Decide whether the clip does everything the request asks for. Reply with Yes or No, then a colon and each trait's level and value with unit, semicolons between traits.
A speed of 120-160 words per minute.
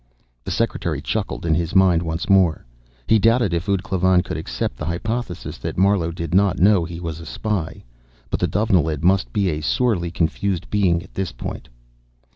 No: average, 185 wpm